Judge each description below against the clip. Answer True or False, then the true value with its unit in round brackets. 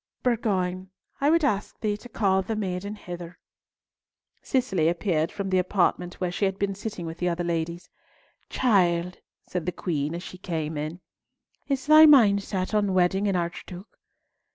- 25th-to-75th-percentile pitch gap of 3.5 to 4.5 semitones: False (3.1 semitones)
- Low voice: False (185 Hz)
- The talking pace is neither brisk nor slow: True (165 wpm)